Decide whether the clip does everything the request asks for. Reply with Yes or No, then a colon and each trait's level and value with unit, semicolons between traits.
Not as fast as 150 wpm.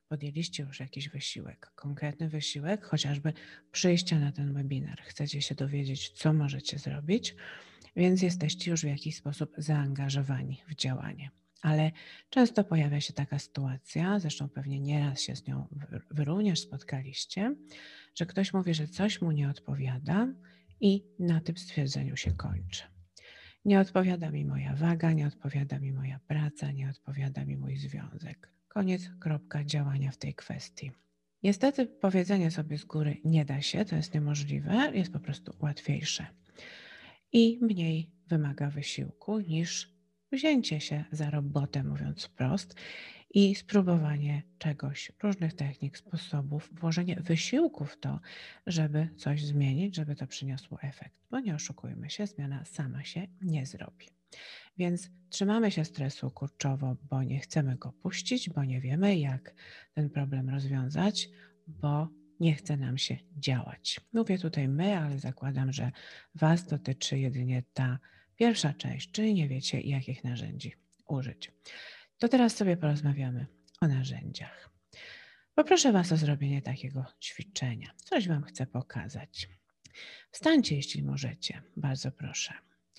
Yes: average, 135 wpm